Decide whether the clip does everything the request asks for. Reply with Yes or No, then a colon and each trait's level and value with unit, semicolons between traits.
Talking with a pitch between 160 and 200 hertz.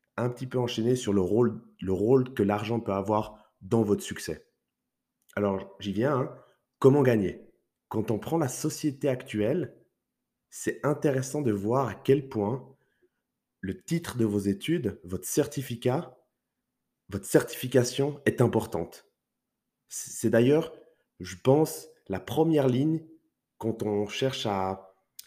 No: low, 120 Hz